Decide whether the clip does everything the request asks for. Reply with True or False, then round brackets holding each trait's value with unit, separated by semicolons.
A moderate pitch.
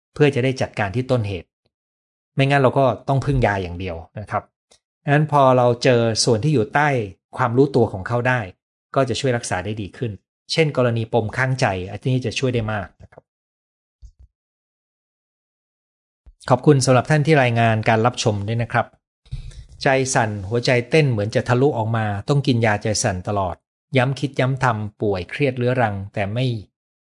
False (120 Hz)